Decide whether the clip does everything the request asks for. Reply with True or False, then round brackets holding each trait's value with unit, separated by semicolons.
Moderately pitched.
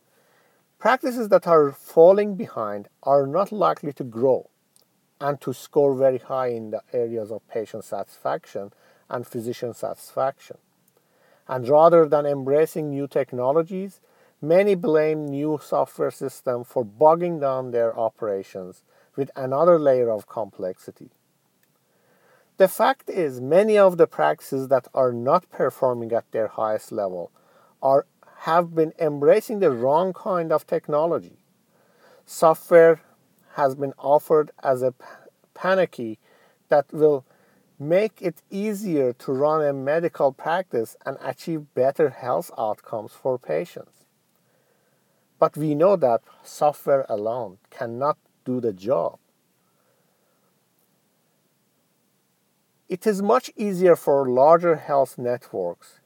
True (145 Hz)